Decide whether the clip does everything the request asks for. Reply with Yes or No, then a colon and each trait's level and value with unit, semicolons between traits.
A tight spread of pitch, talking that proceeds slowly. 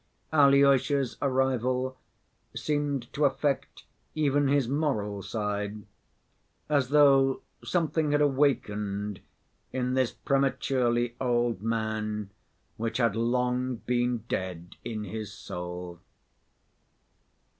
No: average, 4.4 semitones; slow, 90 wpm